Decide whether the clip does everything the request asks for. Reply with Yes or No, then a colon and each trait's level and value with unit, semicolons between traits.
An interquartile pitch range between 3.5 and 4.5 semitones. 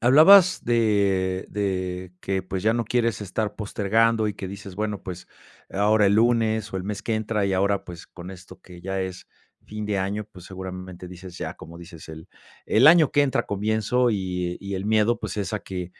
No: average, 2.9 semitones